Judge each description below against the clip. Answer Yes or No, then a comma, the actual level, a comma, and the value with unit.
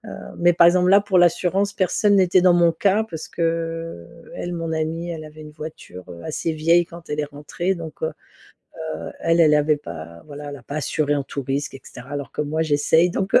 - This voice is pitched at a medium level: Yes, medium, 160 Hz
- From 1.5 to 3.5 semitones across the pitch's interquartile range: Yes, average, 2.9 semitones